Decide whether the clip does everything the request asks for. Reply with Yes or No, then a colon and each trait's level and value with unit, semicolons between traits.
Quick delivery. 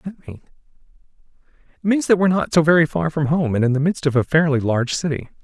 Yes: fast, 210 wpm